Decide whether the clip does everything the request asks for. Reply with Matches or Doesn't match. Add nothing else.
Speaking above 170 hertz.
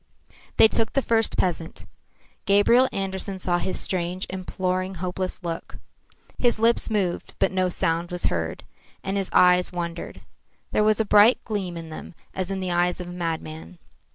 Matches